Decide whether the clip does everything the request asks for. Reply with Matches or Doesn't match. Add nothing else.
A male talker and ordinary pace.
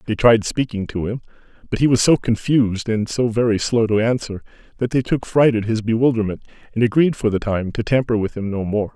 Doesn't match